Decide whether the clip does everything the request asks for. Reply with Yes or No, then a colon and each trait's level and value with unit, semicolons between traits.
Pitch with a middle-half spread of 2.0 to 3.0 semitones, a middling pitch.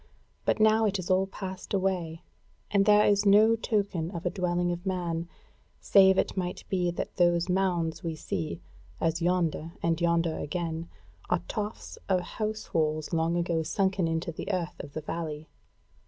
Yes: average, 2.7 semitones; medium, 175 Hz